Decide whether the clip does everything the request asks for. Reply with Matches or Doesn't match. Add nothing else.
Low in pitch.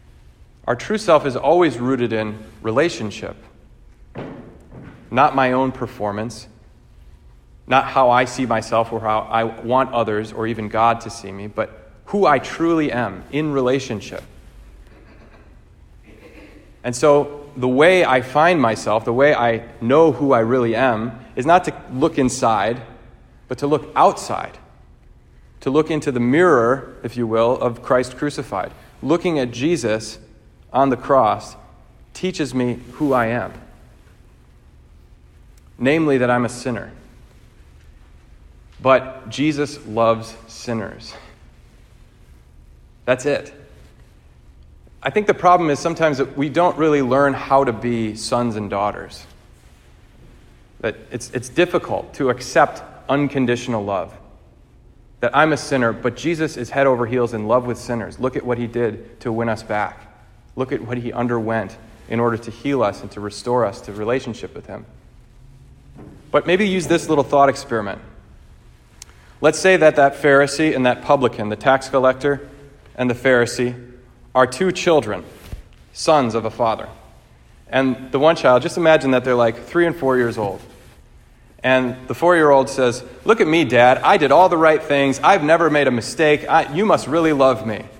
Matches